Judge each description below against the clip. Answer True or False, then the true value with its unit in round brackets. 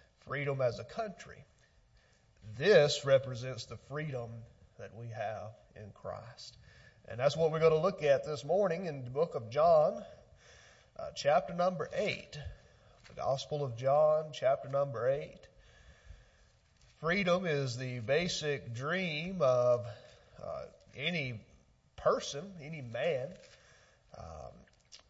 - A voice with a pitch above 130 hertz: True (140 Hz)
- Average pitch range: True (4.6 semitones)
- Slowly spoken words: True (120 wpm)